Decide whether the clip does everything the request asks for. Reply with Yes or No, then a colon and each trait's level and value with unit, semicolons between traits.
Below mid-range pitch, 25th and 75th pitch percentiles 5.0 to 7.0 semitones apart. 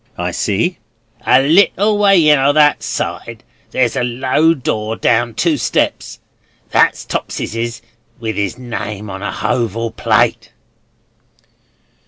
Yes: low, 120 Hz; average, 5.3 semitones